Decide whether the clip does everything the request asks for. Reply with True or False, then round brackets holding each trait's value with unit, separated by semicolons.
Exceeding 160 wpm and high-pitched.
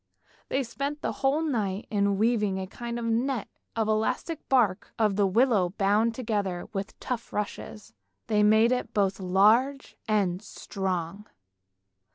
False (150 wpm; 215 Hz)